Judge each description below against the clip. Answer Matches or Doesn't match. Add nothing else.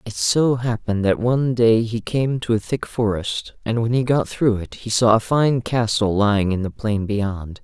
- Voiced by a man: Matches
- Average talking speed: Doesn't match